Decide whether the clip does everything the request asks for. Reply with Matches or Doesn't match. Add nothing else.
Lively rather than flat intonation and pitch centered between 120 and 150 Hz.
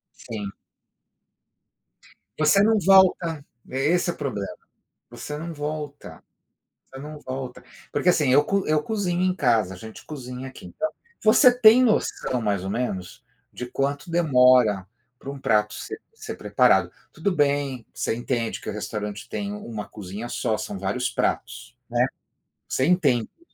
Matches